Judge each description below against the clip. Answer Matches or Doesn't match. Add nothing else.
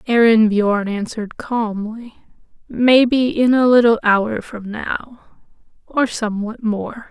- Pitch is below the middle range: Doesn't match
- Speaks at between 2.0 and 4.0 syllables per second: Matches